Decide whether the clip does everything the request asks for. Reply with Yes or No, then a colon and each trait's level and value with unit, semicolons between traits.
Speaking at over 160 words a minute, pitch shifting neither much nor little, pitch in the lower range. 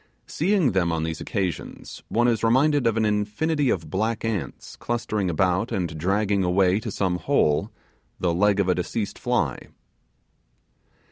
No: average, 150 wpm; average, 4.2 semitones; low, 100 Hz